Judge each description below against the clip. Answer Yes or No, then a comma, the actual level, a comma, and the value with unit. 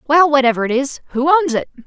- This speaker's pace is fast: Yes, fast, 225 wpm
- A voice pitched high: Yes, very high, 280 Hz